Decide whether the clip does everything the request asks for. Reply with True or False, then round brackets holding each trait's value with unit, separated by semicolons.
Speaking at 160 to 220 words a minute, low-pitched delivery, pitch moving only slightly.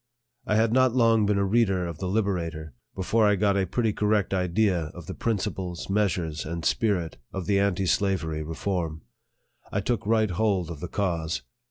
False (185 wpm; 95 Hz; 3.7 semitones)